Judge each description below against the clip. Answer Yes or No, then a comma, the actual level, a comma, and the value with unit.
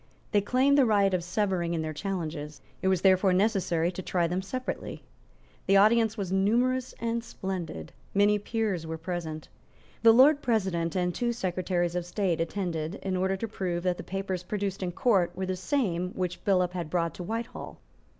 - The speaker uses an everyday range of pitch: Yes, average, 3.1 semitones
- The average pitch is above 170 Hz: Yes, medium, 185 Hz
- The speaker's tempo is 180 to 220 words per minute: Yes, average, 185 wpm